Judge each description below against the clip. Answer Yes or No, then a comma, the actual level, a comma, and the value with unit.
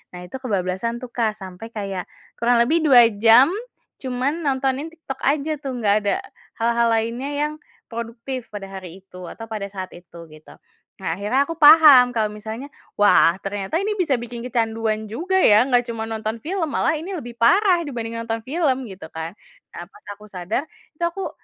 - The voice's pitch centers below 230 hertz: No, high, 235 Hz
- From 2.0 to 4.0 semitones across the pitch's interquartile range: No, average, 4.9 semitones